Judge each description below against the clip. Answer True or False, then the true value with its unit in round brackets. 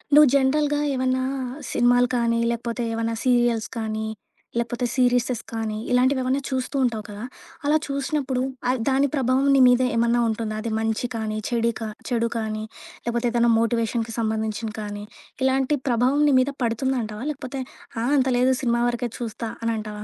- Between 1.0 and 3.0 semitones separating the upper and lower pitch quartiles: True (2.4 semitones)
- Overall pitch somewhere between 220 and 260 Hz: True (240 Hz)